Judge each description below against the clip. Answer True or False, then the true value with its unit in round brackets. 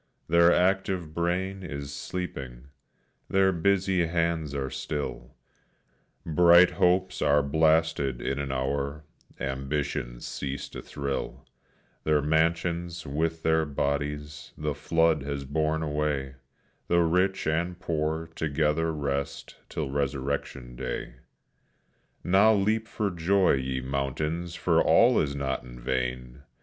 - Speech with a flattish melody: False (3.5 semitones)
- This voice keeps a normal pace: False (115 wpm)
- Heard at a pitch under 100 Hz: True (75 Hz)